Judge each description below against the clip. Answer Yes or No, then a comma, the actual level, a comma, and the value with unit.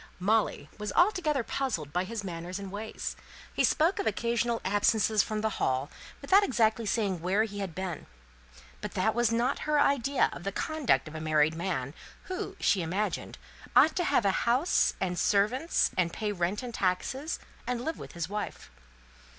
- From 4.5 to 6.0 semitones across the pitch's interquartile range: Yes, average, 5.2 semitones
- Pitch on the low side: No, high, 210 Hz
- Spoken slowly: No, average, 175 wpm